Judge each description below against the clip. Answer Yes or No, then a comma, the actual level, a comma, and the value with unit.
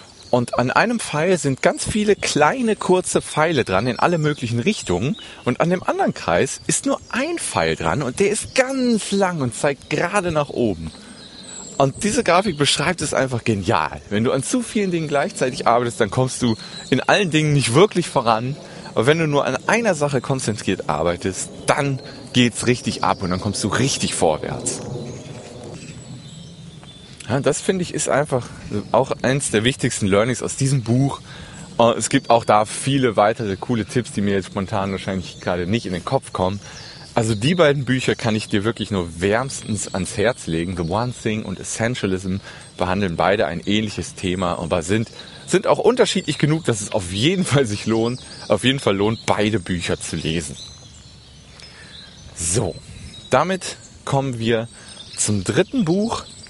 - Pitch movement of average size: No, wide, 6.4 semitones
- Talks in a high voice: No, low, 125 Hz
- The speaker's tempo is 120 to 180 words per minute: Yes, average, 175 wpm